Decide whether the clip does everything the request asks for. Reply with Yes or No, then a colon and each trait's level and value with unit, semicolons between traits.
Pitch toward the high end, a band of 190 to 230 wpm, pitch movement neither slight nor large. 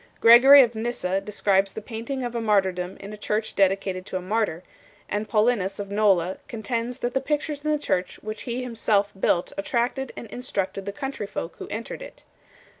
Yes: high, 215 Hz; average, 200 wpm; average, 3.7 semitones